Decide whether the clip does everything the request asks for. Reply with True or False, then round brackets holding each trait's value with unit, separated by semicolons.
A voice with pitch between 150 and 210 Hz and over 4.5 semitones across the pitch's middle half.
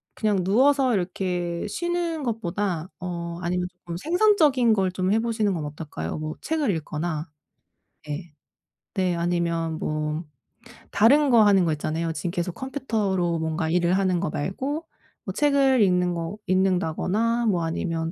True (185 Hz; 5.1 semitones)